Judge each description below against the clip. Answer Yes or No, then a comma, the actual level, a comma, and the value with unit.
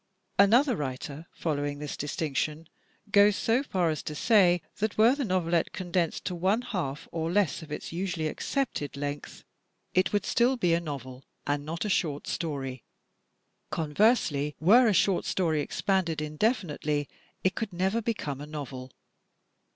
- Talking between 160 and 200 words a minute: No, average, 150 wpm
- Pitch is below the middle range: No, medium, 170 Hz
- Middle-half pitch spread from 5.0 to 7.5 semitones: Yes, wide, 5.4 semitones